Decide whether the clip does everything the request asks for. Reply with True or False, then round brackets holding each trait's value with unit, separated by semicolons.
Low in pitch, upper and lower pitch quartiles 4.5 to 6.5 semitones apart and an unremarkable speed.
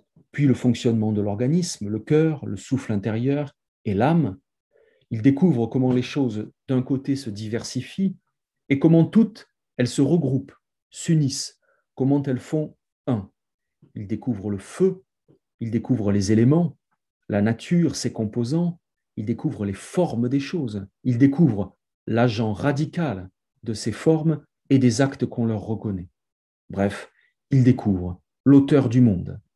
False (130 Hz; 5.1 semitones; 140 wpm)